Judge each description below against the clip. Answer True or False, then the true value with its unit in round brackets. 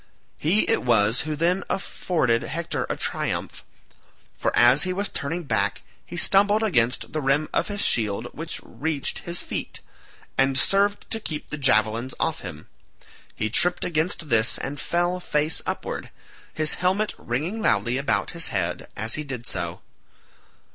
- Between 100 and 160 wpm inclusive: True (155 wpm)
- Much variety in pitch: True (6.7 semitones)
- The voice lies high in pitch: False (150 Hz)